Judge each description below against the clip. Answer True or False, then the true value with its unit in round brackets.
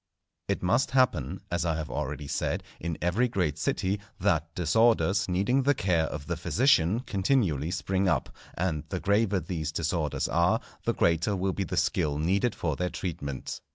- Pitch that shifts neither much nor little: True (4.0 semitones)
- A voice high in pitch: False (90 Hz)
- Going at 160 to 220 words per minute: True (175 wpm)